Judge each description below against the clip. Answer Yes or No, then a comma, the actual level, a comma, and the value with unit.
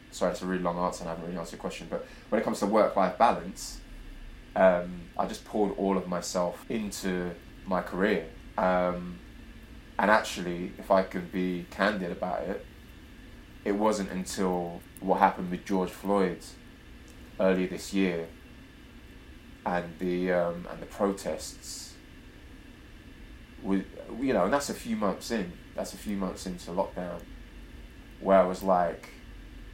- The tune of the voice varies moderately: No, narrow, 1.8 semitones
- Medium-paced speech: Yes, average, 155 wpm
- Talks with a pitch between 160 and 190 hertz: No, very low, 90 Hz